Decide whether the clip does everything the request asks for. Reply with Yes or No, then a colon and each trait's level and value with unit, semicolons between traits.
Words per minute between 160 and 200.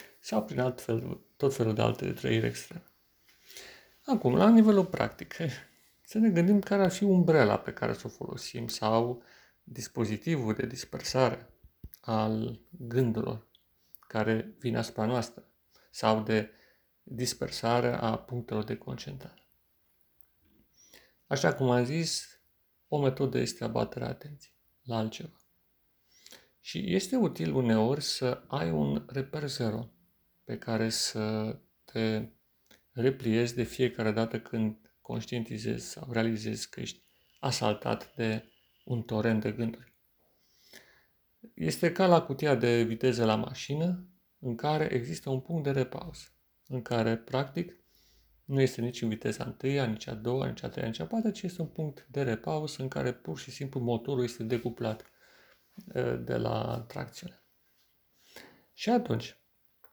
No: average, 135 wpm